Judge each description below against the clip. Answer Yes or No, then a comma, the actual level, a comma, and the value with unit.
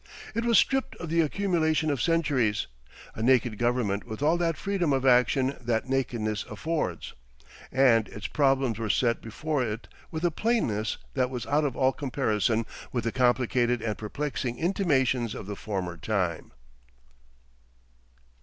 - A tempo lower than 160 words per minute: Yes, average, 150 wpm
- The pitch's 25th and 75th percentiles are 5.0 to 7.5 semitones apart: Yes, average, 5.3 semitones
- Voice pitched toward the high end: No, low, 125 Hz